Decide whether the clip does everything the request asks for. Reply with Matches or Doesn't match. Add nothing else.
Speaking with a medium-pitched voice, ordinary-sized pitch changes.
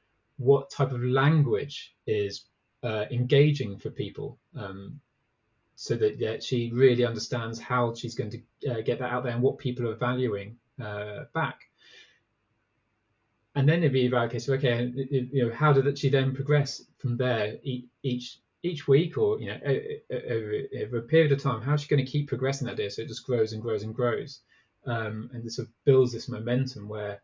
Doesn't match